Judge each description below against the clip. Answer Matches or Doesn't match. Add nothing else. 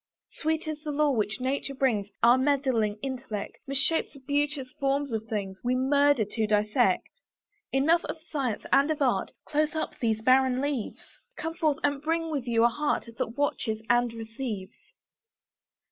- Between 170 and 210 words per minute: Doesn't match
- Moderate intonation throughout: Matches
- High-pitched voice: Matches